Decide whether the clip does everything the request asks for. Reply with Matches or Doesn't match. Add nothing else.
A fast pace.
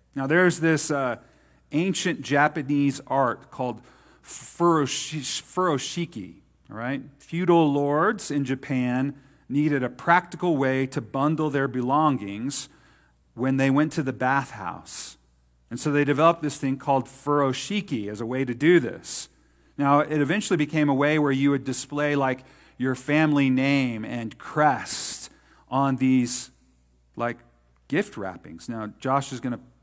Doesn't match